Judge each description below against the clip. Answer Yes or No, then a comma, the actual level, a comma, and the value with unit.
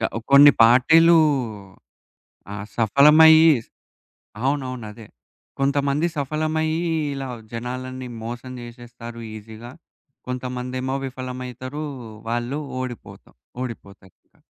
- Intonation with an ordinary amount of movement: Yes, average, 3.0 semitones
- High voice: No, low, 130 Hz